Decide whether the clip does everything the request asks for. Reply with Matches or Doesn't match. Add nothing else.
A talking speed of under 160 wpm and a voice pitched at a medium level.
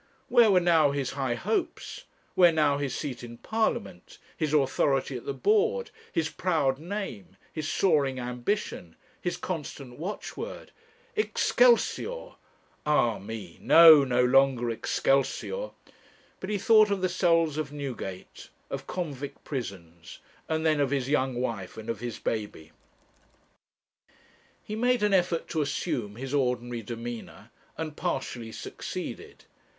Matches